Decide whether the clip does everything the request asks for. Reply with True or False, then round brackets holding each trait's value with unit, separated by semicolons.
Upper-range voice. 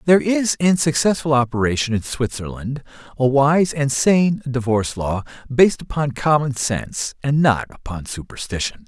False (135 Hz)